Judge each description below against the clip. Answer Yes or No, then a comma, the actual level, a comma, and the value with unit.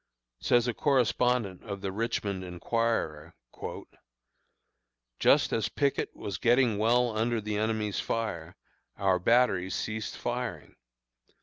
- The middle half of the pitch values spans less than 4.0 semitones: Yes, average, 3.6 semitones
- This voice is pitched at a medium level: No, low, 110 Hz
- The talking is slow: Yes, slow, 110 wpm